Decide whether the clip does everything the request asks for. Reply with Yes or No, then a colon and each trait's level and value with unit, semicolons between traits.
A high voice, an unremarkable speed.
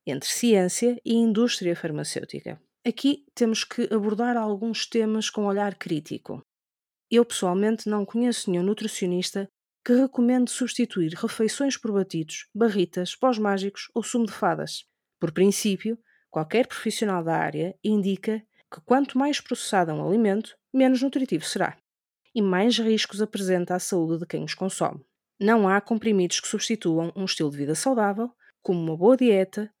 Yes: high, 215 Hz; average, 145 wpm